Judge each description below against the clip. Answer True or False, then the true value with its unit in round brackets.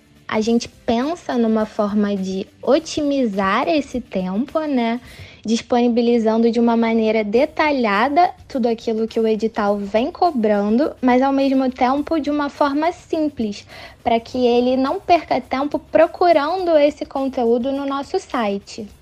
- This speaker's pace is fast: False (135 wpm)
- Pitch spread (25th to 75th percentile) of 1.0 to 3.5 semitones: False (4.7 semitones)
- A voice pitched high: True (245 Hz)